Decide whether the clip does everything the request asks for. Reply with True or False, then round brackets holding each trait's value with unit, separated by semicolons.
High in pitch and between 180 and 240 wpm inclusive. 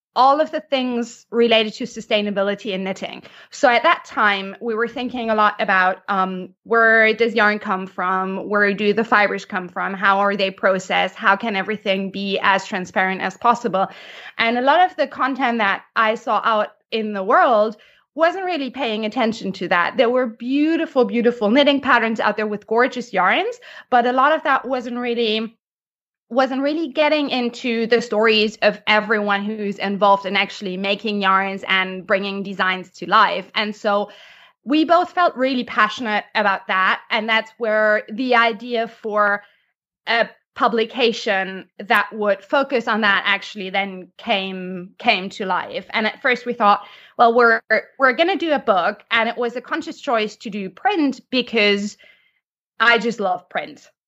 False (220 Hz; 170 wpm)